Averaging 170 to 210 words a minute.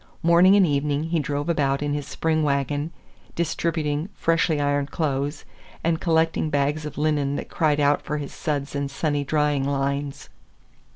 No: average, 160 wpm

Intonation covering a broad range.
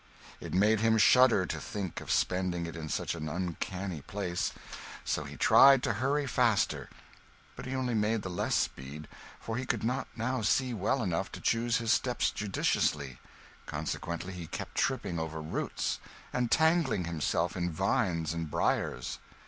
Yes: wide, 5.9 semitones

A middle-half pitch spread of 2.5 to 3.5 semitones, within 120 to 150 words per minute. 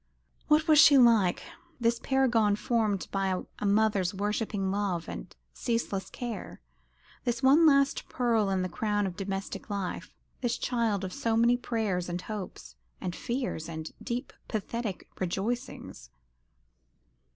No: average, 3.9 semitones; slow, 135 wpm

